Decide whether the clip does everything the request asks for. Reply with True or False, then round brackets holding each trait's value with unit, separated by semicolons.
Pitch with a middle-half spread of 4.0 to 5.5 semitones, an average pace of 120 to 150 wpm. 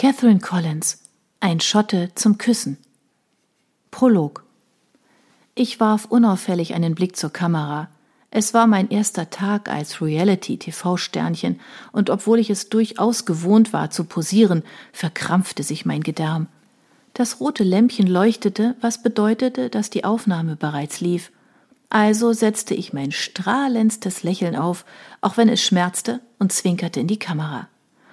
True (4.5 semitones; 130 wpm)